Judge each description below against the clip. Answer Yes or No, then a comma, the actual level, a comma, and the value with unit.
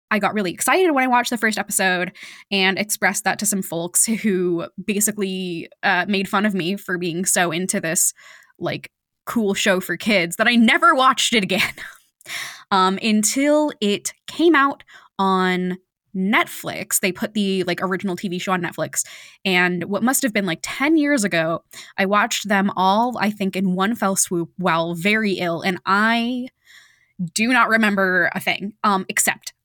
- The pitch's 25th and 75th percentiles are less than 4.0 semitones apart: Yes, average, 3.1 semitones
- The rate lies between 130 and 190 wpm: Yes, average, 175 wpm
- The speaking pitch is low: No, high, 195 Hz